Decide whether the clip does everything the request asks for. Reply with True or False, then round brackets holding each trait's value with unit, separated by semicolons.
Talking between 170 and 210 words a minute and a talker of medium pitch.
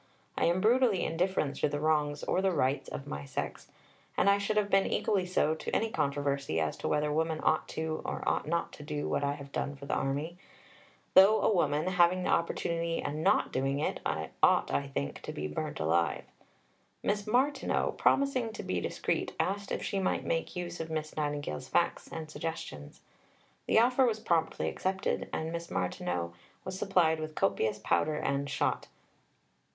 True (180 wpm; 160 Hz)